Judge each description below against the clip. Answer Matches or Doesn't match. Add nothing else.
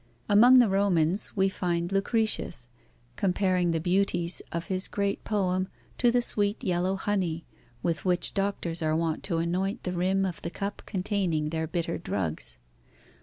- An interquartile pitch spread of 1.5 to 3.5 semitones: Matches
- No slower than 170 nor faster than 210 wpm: Doesn't match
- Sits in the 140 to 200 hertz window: Matches